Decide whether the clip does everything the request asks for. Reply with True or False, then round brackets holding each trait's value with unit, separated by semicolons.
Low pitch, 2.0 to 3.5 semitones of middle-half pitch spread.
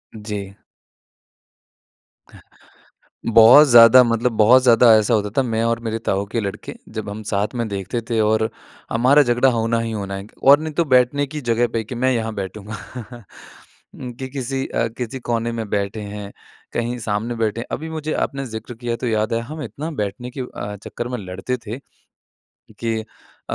True (115 Hz; 2.6 semitones)